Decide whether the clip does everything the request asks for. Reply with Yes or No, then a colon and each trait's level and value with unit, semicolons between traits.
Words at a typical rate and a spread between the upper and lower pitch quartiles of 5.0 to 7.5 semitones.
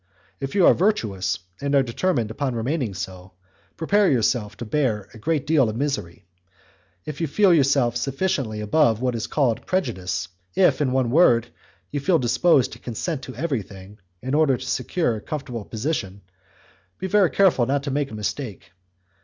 Yes: average, 170 wpm; wide, 5.5 semitones